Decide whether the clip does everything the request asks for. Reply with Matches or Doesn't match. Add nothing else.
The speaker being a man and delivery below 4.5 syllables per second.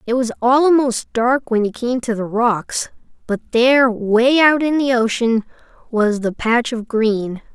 Doesn't match